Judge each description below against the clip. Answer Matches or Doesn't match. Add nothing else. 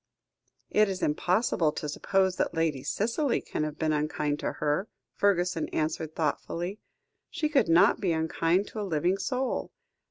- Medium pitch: Matches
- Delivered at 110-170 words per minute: Matches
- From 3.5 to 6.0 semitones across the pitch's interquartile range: Matches